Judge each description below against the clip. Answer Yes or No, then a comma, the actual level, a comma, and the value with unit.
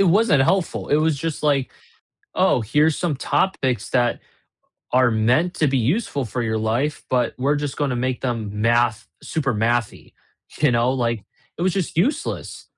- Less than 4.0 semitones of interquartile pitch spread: No, average, 4.4 semitones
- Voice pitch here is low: Yes, low, 130 Hz